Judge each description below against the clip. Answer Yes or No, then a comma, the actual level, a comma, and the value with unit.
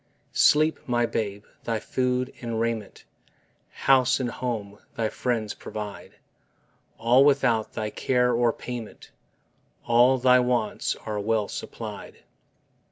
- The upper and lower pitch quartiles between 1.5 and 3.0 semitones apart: Yes, narrow, 2.4 semitones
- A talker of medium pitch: No, low, 120 Hz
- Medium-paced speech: No, slow, 115 wpm